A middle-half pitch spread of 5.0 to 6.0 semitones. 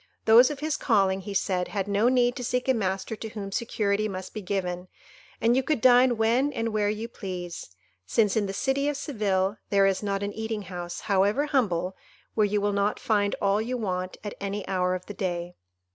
No: average, 3.3 semitones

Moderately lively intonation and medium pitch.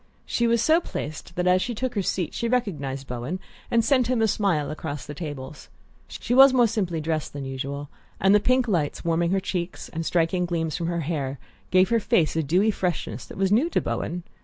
No: wide, 6.3 semitones; medium, 175 Hz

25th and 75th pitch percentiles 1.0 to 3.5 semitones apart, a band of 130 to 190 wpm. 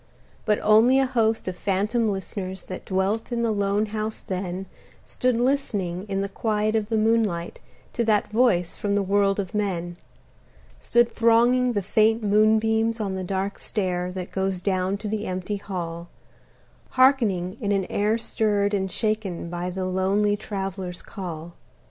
Yes: average, 2.8 semitones; average, 160 wpm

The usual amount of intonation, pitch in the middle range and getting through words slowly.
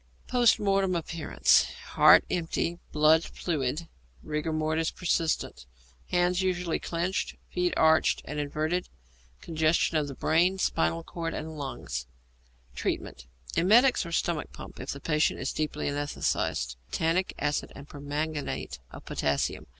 Yes: average, 3.1 semitones; medium, 160 Hz; slow, 125 wpm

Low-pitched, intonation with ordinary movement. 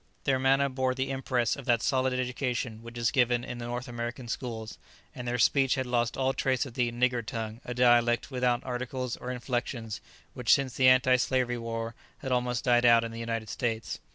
No: low, 125 Hz; narrow, 1.5 semitones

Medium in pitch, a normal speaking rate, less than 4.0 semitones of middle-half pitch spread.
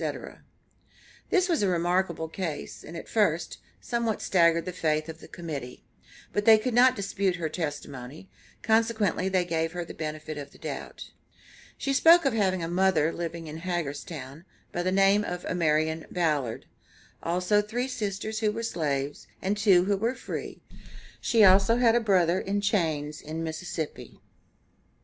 No: medium, 180 Hz; average, 160 wpm; average, 4.5 semitones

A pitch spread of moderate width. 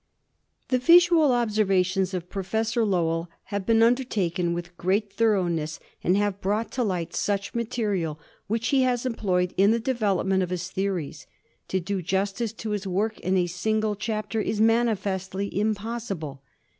Yes: average, 3.4 semitones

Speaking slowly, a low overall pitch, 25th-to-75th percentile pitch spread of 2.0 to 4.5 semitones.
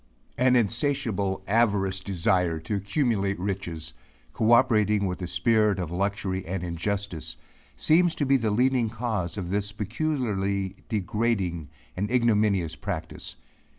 Yes: slow, 120 wpm; low, 100 Hz; average, 3.8 semitones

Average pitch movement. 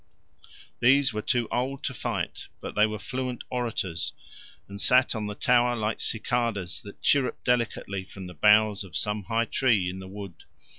Yes: average, 3.6 semitones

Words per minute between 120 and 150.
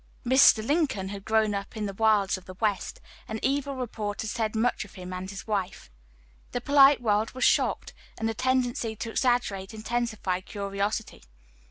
No: average, 175 wpm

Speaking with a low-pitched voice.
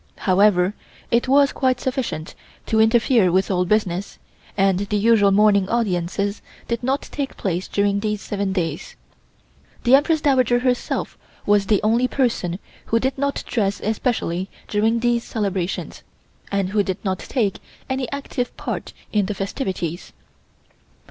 No: high, 210 Hz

